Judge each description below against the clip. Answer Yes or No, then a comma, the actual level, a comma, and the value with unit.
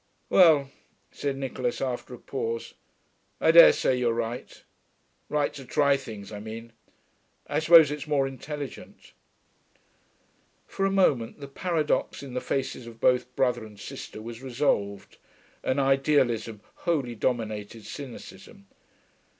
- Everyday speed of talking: No, slow, 130 wpm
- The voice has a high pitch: No, low, 130 Hz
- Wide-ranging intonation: No, average, 3.8 semitones